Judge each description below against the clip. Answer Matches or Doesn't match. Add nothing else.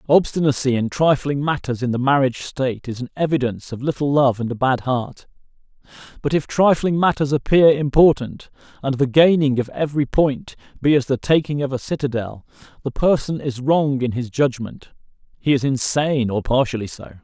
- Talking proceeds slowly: Doesn't match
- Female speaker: Doesn't match